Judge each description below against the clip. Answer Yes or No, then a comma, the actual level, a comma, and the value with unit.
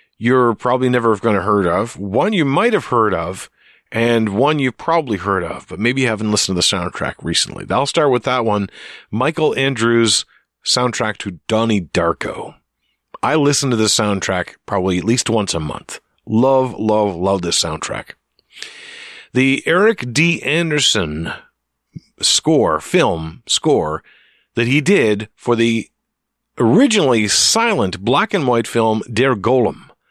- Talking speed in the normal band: Yes, average, 145 wpm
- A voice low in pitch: Yes, low, 115 Hz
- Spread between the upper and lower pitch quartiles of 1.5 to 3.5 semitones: No, average, 4.4 semitones